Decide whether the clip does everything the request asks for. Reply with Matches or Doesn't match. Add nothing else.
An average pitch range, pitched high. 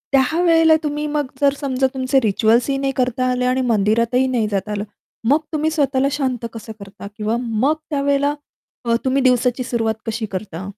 Matches